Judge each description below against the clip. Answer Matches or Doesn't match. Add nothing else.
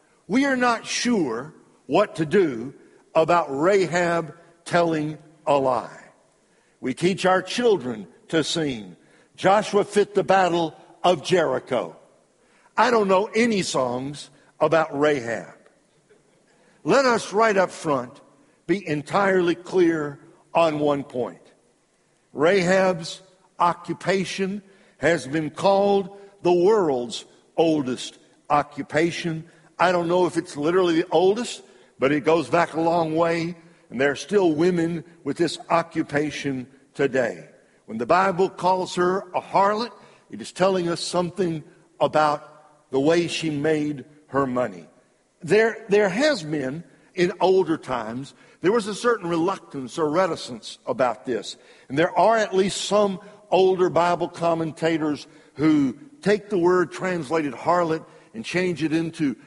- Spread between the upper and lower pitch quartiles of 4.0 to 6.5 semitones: Doesn't match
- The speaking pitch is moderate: Matches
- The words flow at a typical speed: Doesn't match